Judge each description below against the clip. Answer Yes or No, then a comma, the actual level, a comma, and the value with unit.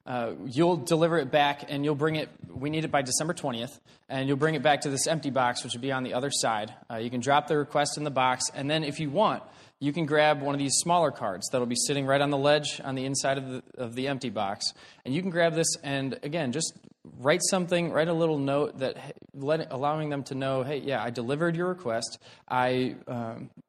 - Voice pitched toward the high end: No, medium, 140 Hz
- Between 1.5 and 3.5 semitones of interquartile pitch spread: Yes, average, 3.1 semitones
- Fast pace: Yes, fast, 245 wpm